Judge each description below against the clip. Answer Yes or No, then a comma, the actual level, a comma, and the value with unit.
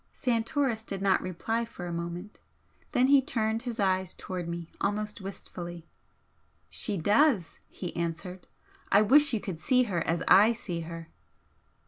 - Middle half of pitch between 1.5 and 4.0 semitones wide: No, average, 4.9 semitones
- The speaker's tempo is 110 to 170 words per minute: Yes, average, 150 wpm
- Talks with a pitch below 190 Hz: No, high, 200 Hz